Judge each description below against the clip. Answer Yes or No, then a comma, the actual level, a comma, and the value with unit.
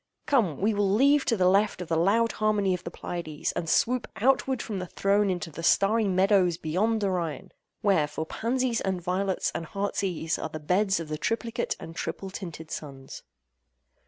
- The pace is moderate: Yes, average, 190 wpm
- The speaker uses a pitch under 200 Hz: Yes, high, 190 Hz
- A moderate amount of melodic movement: Yes, average, 4.3 semitones